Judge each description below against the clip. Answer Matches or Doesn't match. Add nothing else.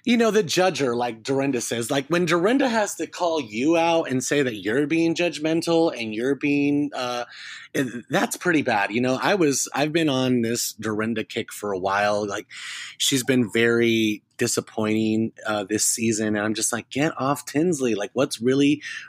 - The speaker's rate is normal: Matches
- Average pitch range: Doesn't match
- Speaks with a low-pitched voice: Matches